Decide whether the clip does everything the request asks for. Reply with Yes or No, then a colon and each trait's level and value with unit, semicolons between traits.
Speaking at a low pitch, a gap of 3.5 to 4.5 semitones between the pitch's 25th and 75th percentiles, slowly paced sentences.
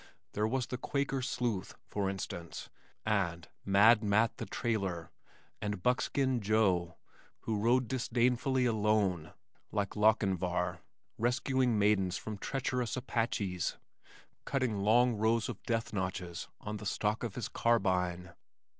Yes: low, 110 Hz; average, 3.9 semitones; slow, 120 wpm